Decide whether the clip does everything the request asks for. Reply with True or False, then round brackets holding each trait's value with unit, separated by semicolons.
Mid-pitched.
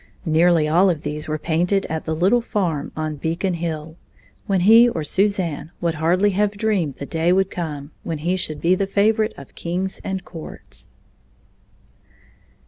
True (170 Hz)